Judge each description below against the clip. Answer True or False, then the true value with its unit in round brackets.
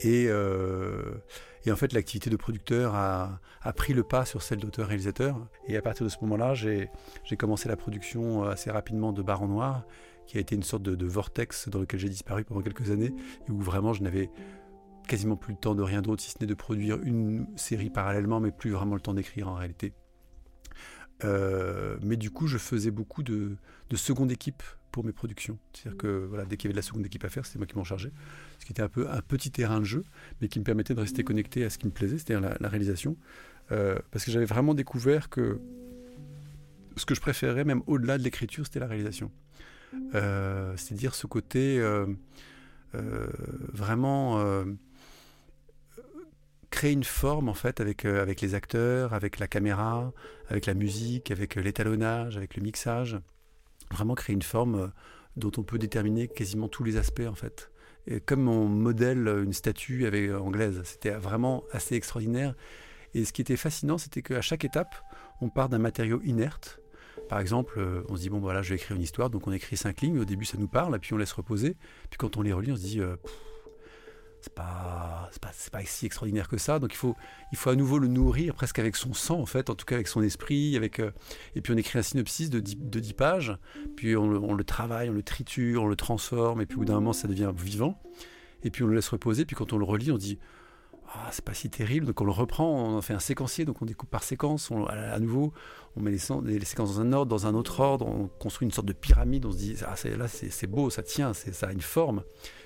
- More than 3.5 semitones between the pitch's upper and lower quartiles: True (3.9 semitones)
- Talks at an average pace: False (225 wpm)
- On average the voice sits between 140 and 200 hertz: False (110 Hz)